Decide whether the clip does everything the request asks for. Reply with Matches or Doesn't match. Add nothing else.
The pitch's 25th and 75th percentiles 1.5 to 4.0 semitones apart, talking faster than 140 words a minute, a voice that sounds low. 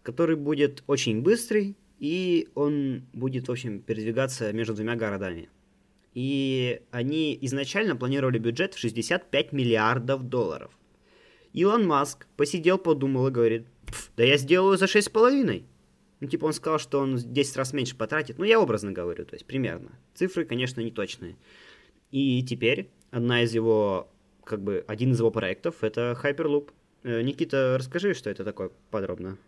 Doesn't match